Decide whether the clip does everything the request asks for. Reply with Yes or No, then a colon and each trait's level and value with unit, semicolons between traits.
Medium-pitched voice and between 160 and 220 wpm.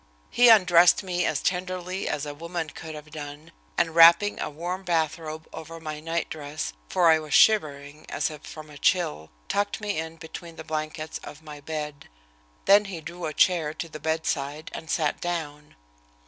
Yes: medium, 160 Hz; average, 175 wpm